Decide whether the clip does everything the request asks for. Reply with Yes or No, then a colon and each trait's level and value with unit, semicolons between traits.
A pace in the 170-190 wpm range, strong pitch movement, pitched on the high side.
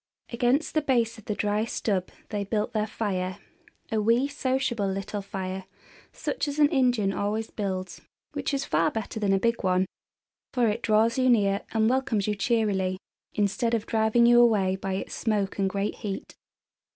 No: average, 175 wpm; average, 3.2 semitones; high, 215 Hz